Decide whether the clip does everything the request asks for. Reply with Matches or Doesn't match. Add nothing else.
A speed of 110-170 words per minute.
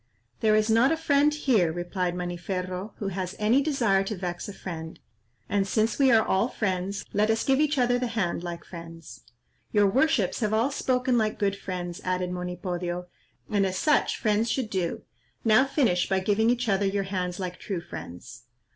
Doesn't match